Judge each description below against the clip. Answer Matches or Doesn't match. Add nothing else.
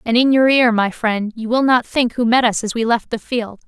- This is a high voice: Matches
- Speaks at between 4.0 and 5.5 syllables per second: Matches